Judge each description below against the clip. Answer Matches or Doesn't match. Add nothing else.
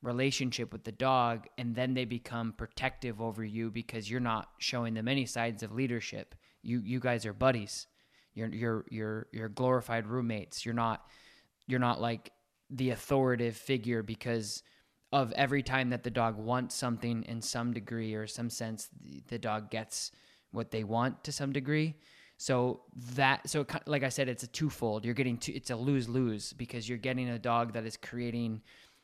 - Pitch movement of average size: Doesn't match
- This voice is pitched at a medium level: Doesn't match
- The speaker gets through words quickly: Doesn't match